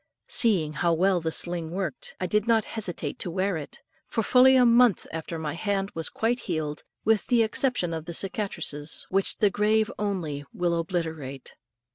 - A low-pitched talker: No, medium, 185 Hz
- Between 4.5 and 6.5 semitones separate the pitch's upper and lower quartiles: Yes, average, 4.8 semitones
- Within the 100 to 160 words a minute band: No, average, 175 wpm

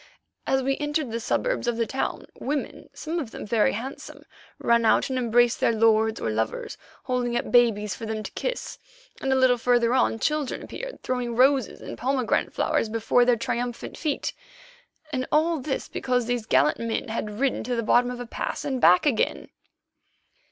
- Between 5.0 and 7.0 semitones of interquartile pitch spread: No, average, 2.7 semitones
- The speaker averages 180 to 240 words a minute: Yes, average, 185 wpm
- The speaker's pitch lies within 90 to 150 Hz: No, high, 245 Hz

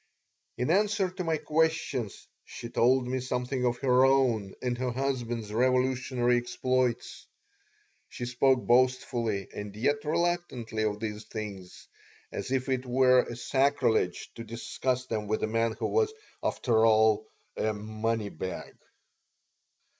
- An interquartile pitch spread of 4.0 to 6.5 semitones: No, average, 3.0 semitones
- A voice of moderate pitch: No, low, 125 Hz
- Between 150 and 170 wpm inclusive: No, slow, 135 wpm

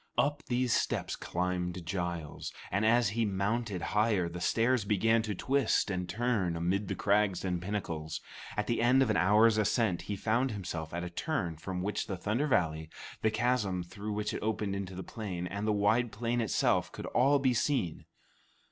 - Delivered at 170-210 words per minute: Yes, average, 185 wpm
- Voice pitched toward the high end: No, low, 105 Hz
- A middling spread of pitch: Yes, average, 4.2 semitones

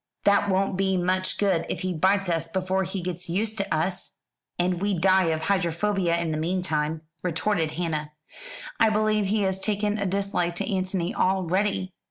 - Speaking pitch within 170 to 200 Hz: Yes, medium, 185 Hz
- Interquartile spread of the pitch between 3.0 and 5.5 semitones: No, narrow, 2.6 semitones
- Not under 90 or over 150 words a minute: No, average, 175 wpm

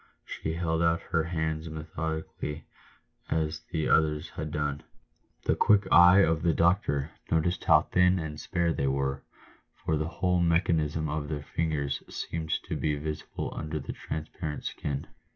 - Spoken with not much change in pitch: Yes, narrow, 1.8 semitones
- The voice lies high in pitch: No, very low, 80 Hz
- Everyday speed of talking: Yes, average, 150 wpm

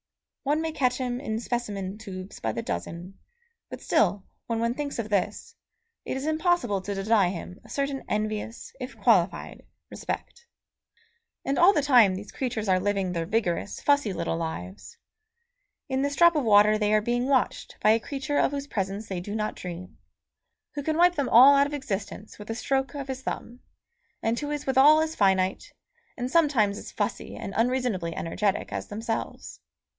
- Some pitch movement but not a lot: No, wide, 5.9 semitones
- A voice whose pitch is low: No, high, 225 Hz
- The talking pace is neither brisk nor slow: Yes, average, 180 wpm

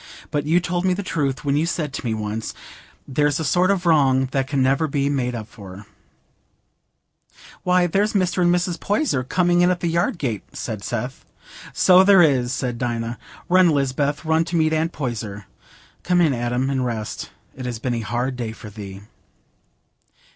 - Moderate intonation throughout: No, wide, 6.1 semitones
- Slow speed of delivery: No, average, 185 wpm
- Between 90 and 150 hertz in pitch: Yes, medium, 140 Hz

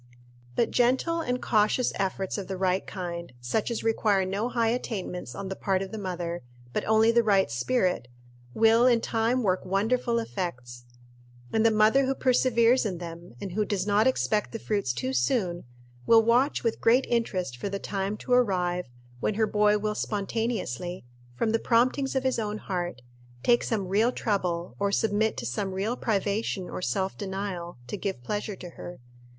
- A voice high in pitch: Yes, high, 205 Hz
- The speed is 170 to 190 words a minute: Yes, average, 180 wpm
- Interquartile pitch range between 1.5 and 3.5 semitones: No, average, 3.9 semitones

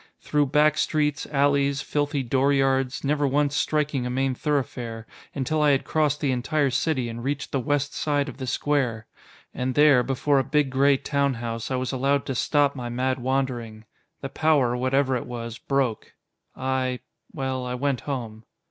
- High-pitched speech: No, low, 135 Hz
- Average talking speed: Yes, average, 175 wpm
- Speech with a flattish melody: Yes, narrow, 2.3 semitones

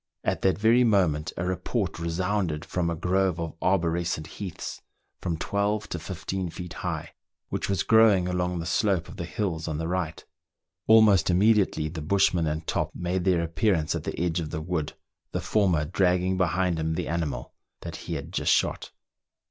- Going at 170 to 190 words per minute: Yes, average, 180 wpm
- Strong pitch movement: No, average, 2.8 semitones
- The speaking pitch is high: No, very low, 90 Hz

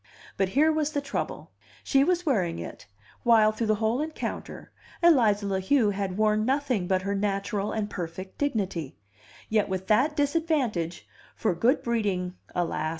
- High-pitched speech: Yes, high, 215 Hz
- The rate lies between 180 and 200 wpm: No, average, 155 wpm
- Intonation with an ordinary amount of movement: No, wide, 6.4 semitones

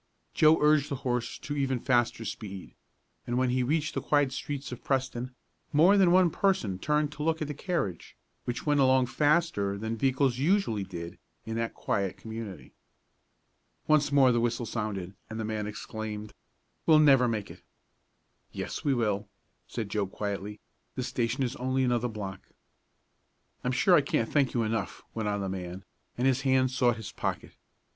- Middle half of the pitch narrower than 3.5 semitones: No, average, 4.8 semitones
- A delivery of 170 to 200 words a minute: Yes, average, 175 wpm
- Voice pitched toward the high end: No, low, 125 Hz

